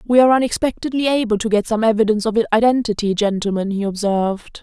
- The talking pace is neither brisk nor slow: Yes, average, 170 wpm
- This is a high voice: Yes, high, 220 Hz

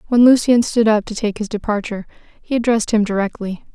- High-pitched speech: Yes, high, 215 Hz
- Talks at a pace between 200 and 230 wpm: No, average, 190 wpm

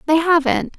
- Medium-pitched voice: No, very high, 315 Hz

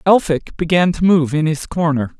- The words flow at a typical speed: Yes, average, 190 wpm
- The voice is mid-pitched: Yes, medium, 160 Hz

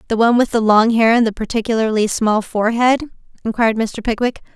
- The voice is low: No, high, 225 Hz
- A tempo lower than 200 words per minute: Yes, average, 185 wpm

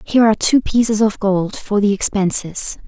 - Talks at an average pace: Yes, average, 190 wpm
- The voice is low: No, high, 210 Hz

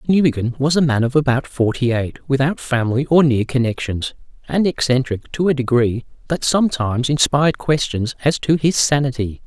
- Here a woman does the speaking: No, male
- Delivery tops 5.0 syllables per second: Yes, 5.4 syllables/s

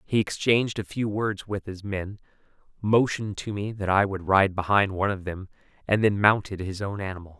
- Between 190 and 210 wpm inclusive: Yes, fast, 205 wpm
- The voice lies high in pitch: No, low, 100 Hz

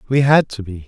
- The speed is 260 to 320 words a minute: Yes, fast, 275 wpm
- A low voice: Yes, low, 120 Hz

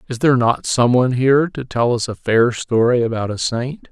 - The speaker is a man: Yes, male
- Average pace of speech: No, fast, 230 wpm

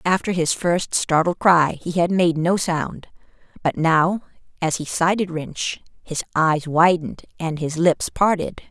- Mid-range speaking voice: Yes, medium, 170 Hz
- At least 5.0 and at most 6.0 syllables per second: No, 4.0 syllables/s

